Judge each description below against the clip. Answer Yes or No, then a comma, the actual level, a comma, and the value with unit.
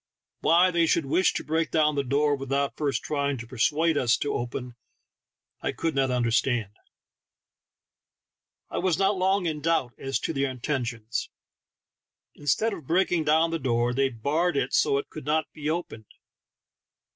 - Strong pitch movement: No, average, 4.2 semitones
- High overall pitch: No, medium, 145 Hz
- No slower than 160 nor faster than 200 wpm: Yes, average, 165 wpm